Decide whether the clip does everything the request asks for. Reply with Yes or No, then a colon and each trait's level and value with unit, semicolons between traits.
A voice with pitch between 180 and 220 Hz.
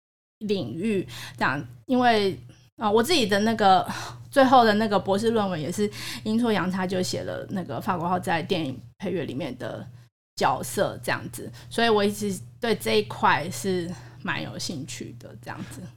Yes: high, 190 Hz